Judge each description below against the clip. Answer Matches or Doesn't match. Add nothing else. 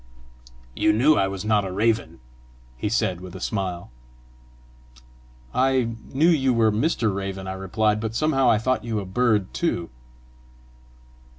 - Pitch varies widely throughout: Doesn't match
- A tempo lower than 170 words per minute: Matches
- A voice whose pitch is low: Matches